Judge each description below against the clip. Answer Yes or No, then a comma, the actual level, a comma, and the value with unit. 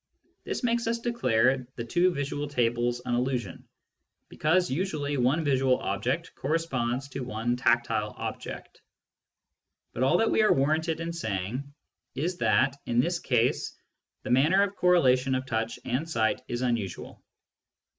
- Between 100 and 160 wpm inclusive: Yes, average, 145 wpm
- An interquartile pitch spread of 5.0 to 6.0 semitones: Yes, average, 5.3 semitones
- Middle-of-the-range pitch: No, low, 130 Hz